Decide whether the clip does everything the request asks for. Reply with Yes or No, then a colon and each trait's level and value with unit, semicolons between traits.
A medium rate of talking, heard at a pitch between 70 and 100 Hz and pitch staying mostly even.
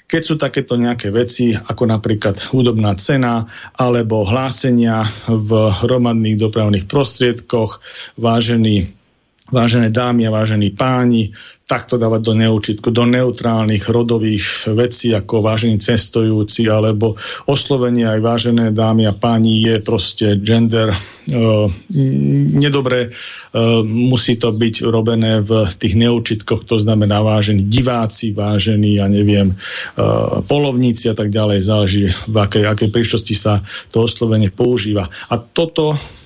No: average, 125 wpm; low, 115 Hz; narrow, 1.9 semitones